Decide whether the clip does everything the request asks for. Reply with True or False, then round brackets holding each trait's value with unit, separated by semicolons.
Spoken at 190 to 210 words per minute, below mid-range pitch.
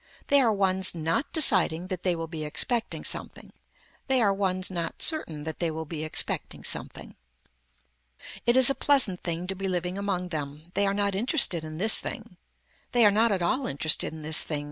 False (195 wpm; 185 Hz)